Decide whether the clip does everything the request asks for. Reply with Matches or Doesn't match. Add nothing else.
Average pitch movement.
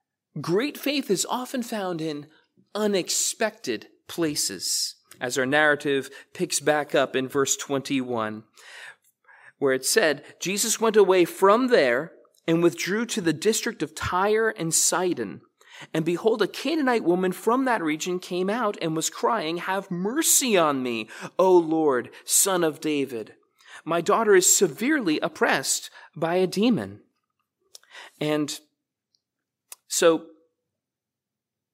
Doesn't match